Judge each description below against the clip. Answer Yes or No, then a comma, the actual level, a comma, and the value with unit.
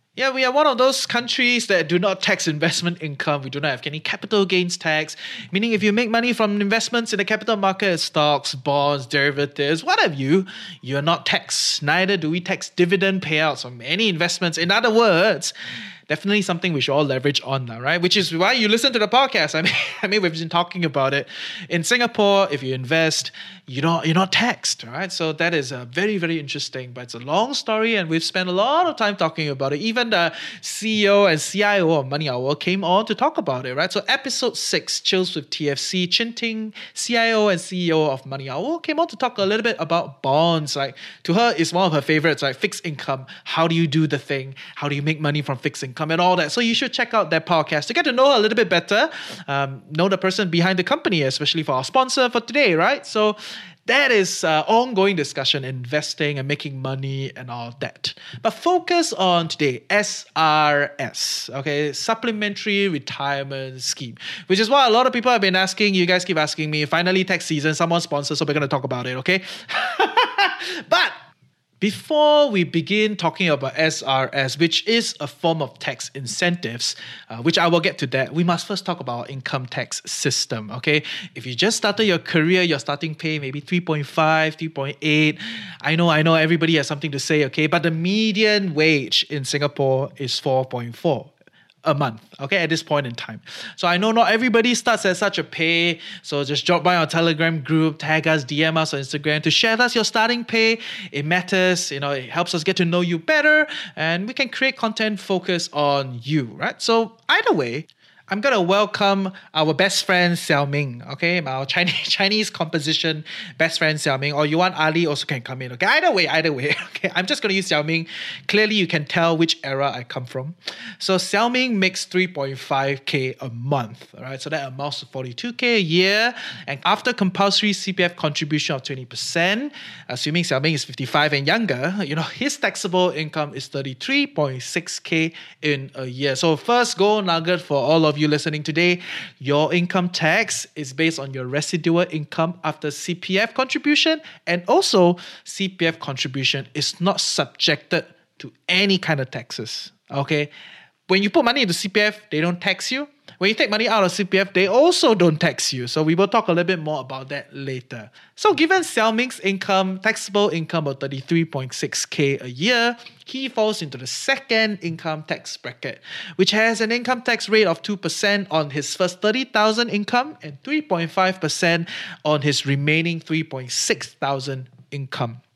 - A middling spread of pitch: No, wide, 5.9 semitones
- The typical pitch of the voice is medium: Yes, medium, 170 Hz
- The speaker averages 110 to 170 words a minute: No, average, 195 wpm